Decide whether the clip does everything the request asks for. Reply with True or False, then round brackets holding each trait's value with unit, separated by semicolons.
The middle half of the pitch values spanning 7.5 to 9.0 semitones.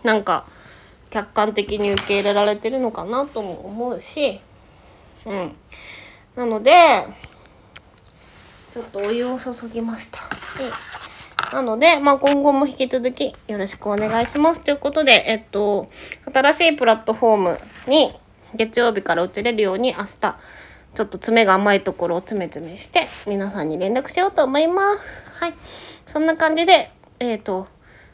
False (5.5 semitones)